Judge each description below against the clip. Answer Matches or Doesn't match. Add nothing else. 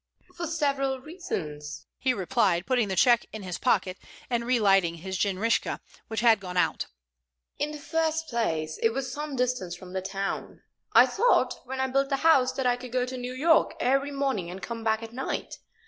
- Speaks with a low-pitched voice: Doesn't match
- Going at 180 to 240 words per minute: Matches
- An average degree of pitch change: Doesn't match